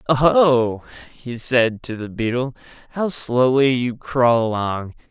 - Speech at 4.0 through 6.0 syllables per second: No, 3.7 syllables/s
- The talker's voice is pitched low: Yes, low, 125 Hz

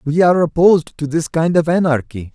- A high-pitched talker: No, medium, 160 Hz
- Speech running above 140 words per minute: Yes, fast, 205 wpm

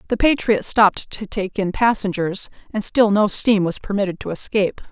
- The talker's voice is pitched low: No, high, 205 Hz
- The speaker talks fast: No, average, 185 wpm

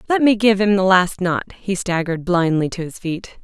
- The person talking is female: Yes, female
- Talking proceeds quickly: Yes, fast, 225 wpm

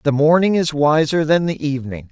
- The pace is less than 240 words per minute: Yes, average, 200 wpm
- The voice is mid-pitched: Yes, medium, 150 Hz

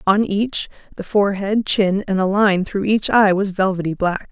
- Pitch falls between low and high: No, high, 195 Hz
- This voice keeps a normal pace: Yes, average, 195 wpm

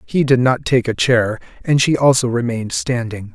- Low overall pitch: Yes, low, 125 Hz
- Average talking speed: Yes, average, 195 wpm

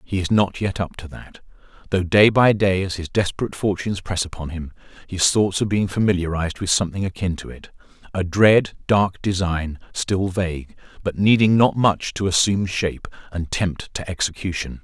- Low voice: Yes, very low, 95 Hz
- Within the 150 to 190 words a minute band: Yes, average, 180 wpm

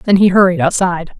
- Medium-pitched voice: Yes, medium, 180 Hz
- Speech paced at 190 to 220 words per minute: Yes, average, 200 wpm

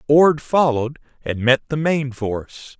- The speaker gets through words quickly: No, average, 150 wpm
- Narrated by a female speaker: No, male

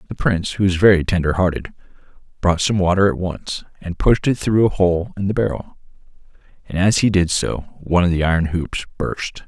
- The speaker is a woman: No, male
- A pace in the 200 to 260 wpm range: Yes, fast, 205 wpm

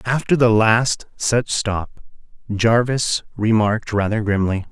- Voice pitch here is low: Yes, low, 110 Hz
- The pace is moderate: No, slow, 115 wpm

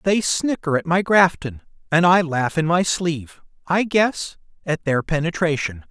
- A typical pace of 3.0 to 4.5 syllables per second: Yes, 4.4 syllables/s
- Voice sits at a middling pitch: Yes, medium, 165 Hz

